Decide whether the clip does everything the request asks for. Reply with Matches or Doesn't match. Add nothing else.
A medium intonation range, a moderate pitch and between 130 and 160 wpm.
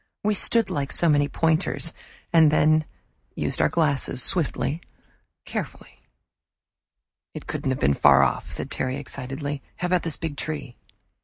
Matches